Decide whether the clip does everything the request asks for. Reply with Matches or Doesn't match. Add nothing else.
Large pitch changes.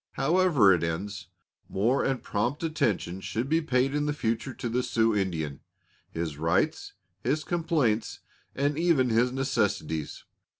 Matches